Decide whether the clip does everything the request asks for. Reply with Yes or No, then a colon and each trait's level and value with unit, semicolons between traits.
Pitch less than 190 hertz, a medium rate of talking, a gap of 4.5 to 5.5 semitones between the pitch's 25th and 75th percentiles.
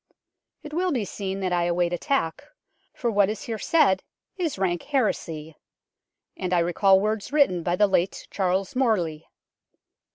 No: high, 195 Hz; average, 155 wpm; average, 5.0 semitones